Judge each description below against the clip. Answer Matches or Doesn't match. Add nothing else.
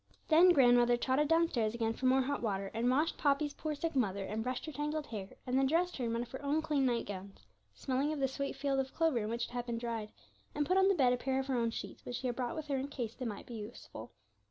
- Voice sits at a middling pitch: Doesn't match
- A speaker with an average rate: Doesn't match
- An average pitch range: Matches